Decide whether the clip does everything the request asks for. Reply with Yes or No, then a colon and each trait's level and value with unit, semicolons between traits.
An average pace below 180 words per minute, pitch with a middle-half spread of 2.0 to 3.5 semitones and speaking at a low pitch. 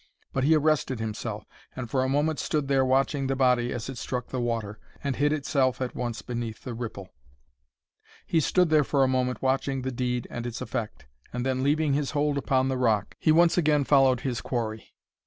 No: fast, 205 wpm; average, 2.8 semitones; low, 130 Hz